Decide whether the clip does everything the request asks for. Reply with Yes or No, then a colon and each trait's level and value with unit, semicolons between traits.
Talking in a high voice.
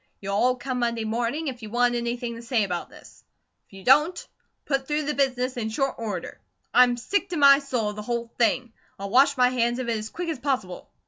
Yes: high, 245 Hz